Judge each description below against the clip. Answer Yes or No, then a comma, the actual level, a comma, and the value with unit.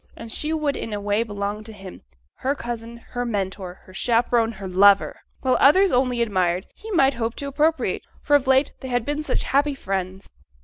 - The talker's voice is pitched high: Yes, high, 235 Hz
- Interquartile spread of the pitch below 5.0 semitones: No, wide, 5.4 semitones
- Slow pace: No, average, 200 wpm